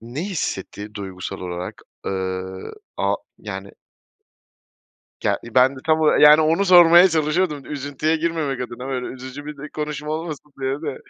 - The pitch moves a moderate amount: Yes, average, 4.1 semitones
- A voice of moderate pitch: Yes, medium, 145 Hz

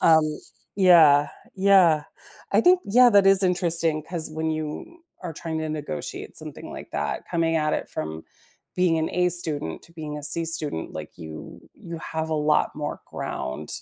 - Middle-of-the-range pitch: Yes, medium, 160 Hz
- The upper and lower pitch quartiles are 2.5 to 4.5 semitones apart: Yes, average, 2.9 semitones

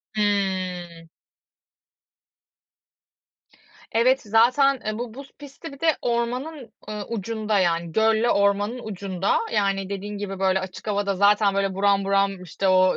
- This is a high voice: Yes, high, 205 Hz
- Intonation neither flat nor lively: Yes, average, 3.0 semitones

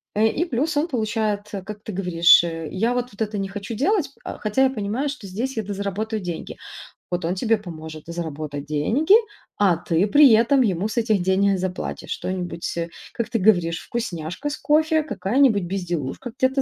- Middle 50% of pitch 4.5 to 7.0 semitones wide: Yes, wide, 5.4 semitones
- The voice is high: Yes, high, 205 Hz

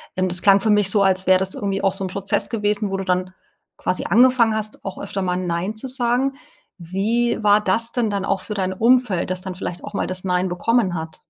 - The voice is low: No, high, 195 Hz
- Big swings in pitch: No, average, 2.9 semitones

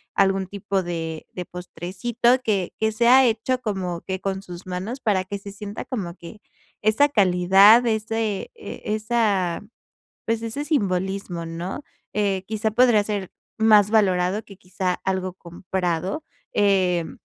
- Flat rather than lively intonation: No, average, 3.2 semitones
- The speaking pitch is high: Yes, high, 195 Hz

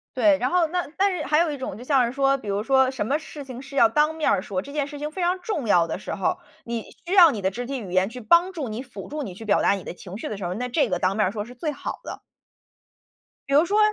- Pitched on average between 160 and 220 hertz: No, very high, 260 Hz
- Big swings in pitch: Yes, wide, 6.4 semitones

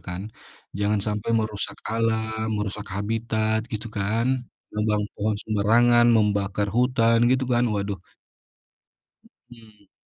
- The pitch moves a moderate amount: No, narrow, 1.8 semitones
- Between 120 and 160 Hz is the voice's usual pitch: No, low, 110 Hz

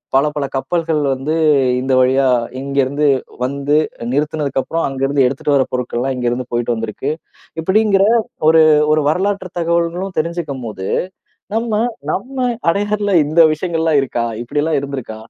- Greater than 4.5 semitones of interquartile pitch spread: No, average, 4.2 semitones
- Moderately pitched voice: Yes, medium, 150 Hz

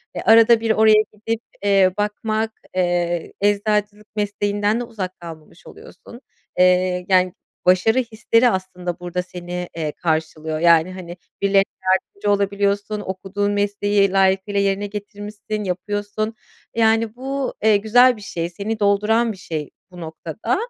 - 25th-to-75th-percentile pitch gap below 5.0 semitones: Yes, average, 2.9 semitones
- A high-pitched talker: Yes, high, 200 Hz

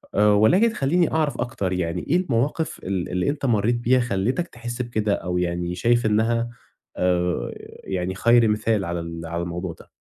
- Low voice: Yes, low, 110 Hz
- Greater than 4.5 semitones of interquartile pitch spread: Yes, average, 5.3 semitones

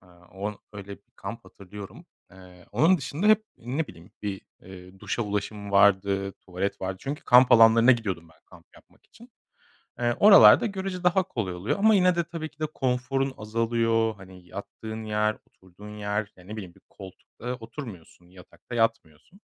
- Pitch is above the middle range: No, low, 105 Hz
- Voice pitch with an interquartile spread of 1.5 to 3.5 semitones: No, average, 5.1 semitones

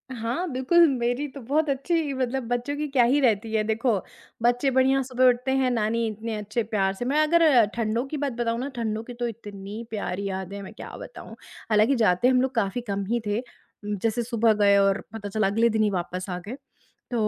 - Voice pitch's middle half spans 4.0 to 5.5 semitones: No, average, 3.6 semitones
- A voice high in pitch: Yes, high, 235 Hz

